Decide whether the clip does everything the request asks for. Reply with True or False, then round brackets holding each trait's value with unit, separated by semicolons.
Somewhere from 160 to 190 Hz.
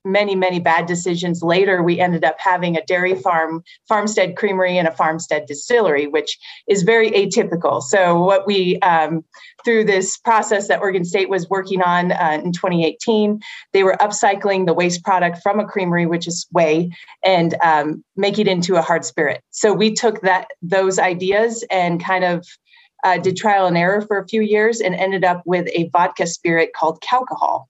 True (185 Hz)